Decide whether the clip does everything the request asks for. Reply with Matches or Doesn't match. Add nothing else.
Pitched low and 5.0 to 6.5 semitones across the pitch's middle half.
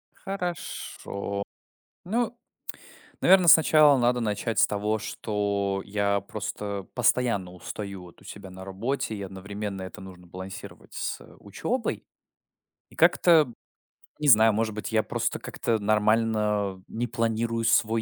Doesn't match